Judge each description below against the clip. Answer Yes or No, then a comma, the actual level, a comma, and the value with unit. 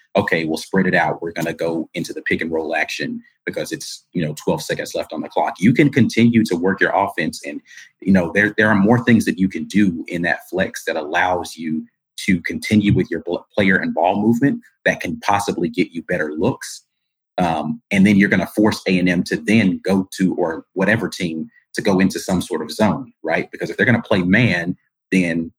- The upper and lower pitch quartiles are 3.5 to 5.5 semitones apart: Yes, average, 4.4 semitones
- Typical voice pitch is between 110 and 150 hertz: No, very low, 95 Hz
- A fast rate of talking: Yes, fast, 220 wpm